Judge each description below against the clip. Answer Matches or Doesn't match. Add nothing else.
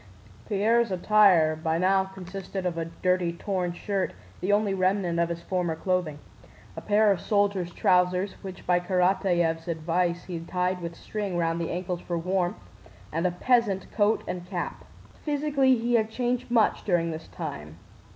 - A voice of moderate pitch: Matches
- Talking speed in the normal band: Matches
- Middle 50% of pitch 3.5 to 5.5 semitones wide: Doesn't match